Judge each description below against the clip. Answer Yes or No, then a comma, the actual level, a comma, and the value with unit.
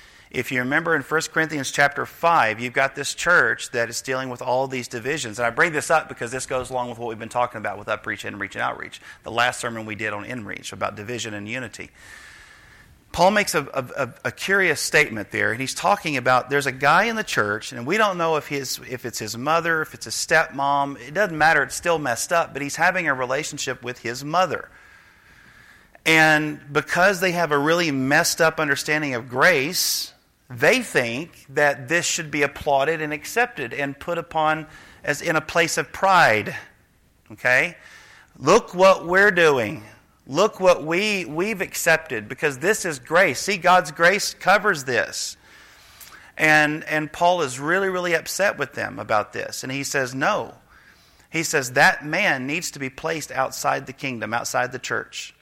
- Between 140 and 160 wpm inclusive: No, average, 190 wpm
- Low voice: No, medium, 145 Hz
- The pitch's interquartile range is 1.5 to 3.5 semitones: No, average, 4.8 semitones